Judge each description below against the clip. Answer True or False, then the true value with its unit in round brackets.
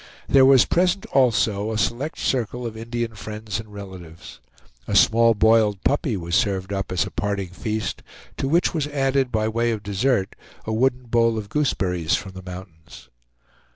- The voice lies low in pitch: True (110 Hz)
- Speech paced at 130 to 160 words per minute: False (170 wpm)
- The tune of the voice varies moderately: True (4.1 semitones)